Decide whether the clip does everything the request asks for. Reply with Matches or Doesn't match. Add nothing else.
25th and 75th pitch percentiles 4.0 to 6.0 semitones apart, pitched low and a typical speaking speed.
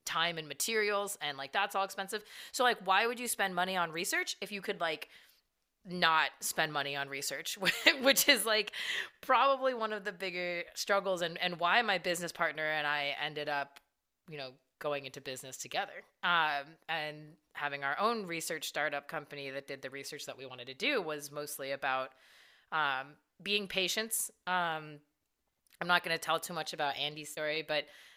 Doesn't match